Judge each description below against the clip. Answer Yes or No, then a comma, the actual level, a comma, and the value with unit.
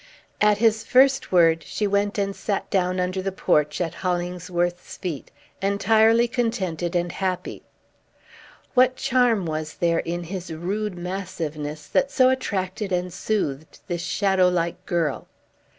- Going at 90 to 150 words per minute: Yes, slow, 135 wpm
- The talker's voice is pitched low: No, medium, 185 Hz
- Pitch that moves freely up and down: No, average, 3.3 semitones